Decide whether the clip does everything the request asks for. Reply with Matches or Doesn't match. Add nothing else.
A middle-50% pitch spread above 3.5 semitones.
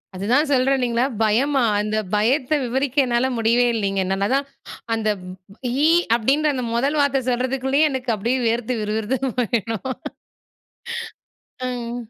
Doesn't match